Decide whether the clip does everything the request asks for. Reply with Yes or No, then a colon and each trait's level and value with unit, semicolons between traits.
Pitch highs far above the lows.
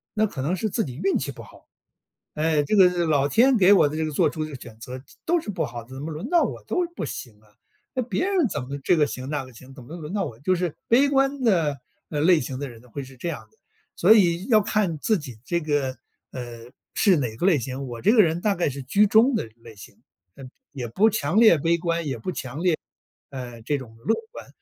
Yes: wide, 7.2 semitones